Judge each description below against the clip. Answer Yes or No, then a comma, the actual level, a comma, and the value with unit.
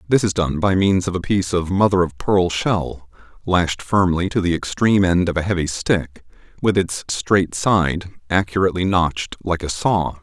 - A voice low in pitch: Yes, very low, 90 Hz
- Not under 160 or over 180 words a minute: No, average, 190 wpm